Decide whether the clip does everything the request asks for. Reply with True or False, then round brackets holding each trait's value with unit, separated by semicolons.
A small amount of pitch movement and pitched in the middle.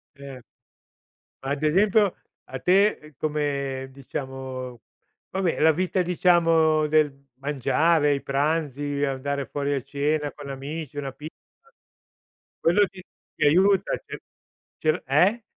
False (3.1 semitones; 150 Hz)